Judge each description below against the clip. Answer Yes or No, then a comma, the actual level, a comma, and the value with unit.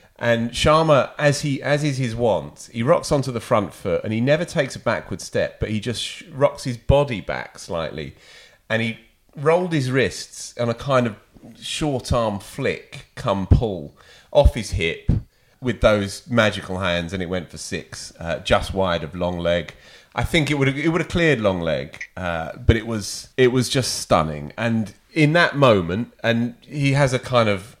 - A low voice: Yes, low, 120 Hz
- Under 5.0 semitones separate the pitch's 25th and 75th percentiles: No, wide, 5.6 semitones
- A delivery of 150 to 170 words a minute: No, average, 195 wpm